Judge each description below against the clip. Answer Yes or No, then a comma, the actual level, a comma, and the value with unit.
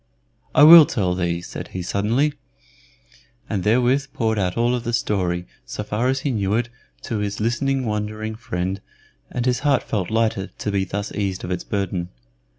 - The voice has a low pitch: Yes, low, 105 Hz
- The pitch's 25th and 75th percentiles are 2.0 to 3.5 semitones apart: No, average, 4.0 semitones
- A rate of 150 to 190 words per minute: Yes, average, 180 wpm